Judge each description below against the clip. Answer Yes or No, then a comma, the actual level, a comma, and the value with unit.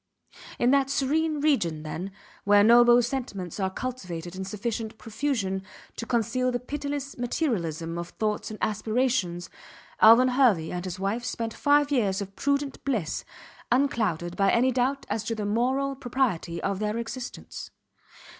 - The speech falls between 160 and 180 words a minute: No, average, 145 wpm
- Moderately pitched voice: No, high, 230 Hz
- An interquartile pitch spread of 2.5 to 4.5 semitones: No, average, 5.2 semitones